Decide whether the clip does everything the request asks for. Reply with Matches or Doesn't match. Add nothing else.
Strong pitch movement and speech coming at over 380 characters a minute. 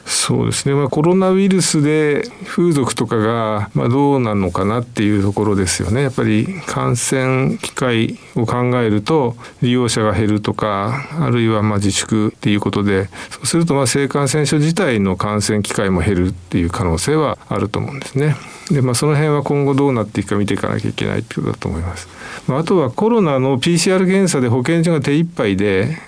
Matches